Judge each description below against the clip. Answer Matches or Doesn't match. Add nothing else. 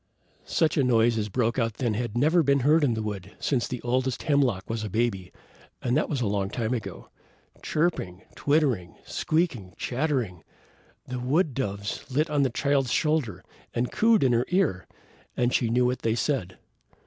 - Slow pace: Doesn't match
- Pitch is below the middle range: Matches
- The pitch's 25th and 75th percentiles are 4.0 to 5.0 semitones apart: Matches